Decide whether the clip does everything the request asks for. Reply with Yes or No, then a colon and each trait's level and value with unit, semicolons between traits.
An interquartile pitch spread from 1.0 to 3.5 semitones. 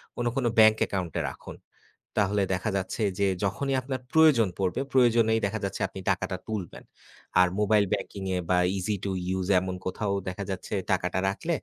Yes: average, 3.1 semitones